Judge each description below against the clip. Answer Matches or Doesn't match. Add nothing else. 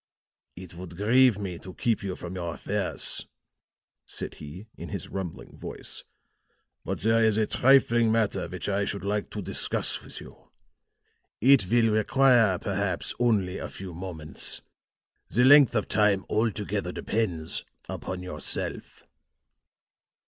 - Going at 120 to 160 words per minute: Matches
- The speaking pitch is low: Matches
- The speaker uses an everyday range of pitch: Matches